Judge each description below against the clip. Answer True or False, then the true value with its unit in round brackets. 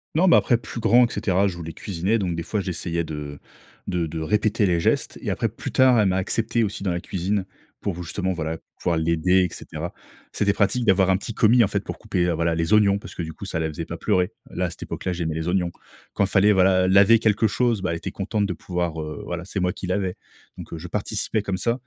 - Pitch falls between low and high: False (95 Hz)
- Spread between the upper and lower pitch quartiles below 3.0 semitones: False (3.4 semitones)